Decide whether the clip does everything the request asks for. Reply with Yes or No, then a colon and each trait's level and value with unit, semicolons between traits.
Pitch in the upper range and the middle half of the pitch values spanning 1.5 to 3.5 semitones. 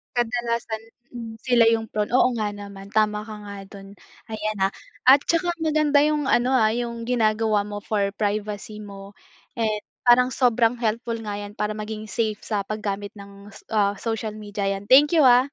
Yes: high, 215 Hz; average, 2.7 semitones